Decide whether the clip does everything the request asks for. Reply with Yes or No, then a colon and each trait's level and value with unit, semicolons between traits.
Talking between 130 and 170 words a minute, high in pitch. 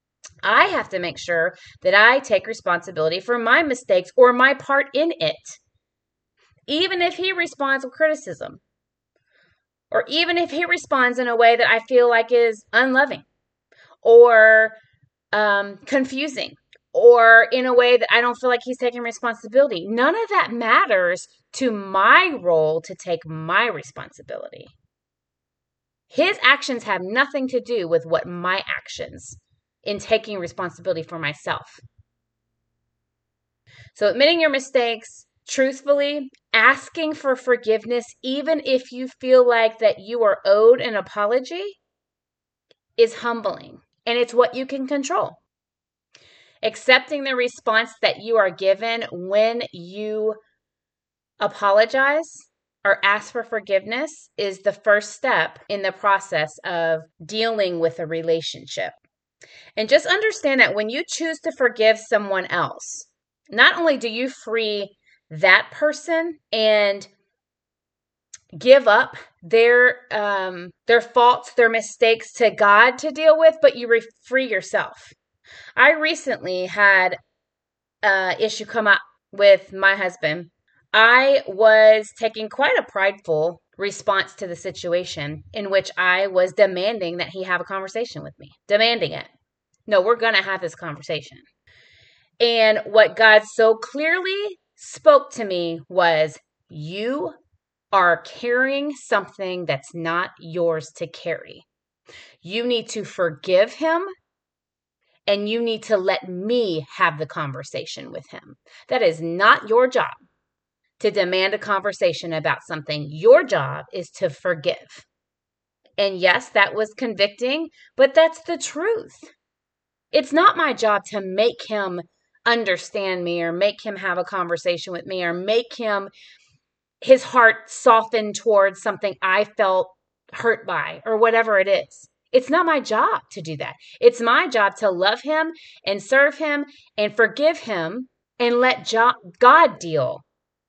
Yes: average, 140 wpm; high, 220 Hz